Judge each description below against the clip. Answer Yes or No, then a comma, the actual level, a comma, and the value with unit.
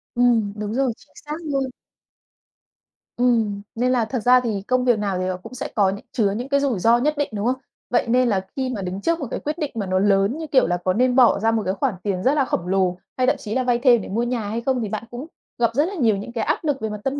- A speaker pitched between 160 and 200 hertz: No, high, 235 Hz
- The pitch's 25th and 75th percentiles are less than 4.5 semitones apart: Yes, average, 4.1 semitones